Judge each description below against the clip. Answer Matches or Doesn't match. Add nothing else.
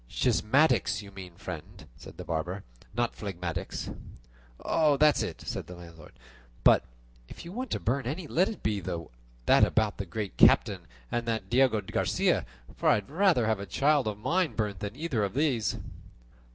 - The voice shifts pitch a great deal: Matches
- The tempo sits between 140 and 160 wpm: Doesn't match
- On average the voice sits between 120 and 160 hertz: Doesn't match